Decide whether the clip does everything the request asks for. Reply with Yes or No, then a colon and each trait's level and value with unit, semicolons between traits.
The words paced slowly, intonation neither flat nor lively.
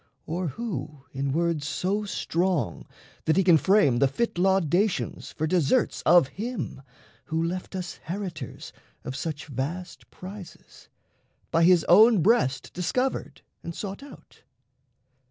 Yes: slow, 130 wpm; average, 4.0 semitones